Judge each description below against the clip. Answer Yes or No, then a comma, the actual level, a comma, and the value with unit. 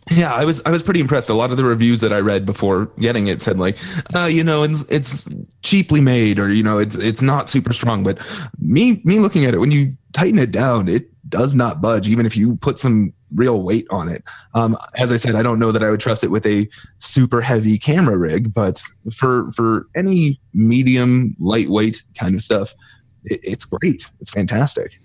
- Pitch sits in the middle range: No, low, 120 Hz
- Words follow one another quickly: Yes, fast, 215 wpm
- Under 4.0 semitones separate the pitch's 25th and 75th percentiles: No, average, 5.0 semitones